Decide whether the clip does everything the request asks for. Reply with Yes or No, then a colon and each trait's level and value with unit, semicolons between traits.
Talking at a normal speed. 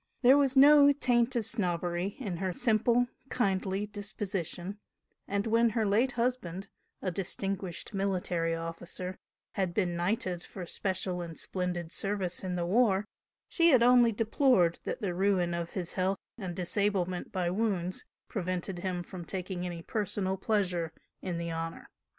Yes: average, 150 wpm